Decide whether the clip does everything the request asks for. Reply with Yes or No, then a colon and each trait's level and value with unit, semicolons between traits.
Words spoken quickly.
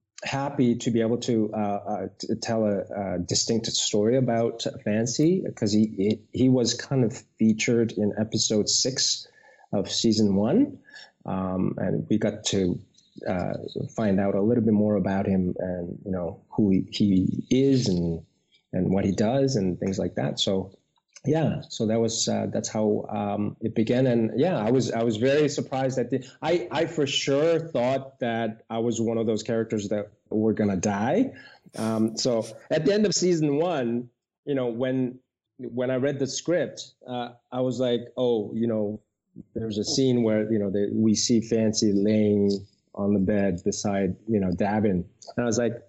No: average, 180 wpm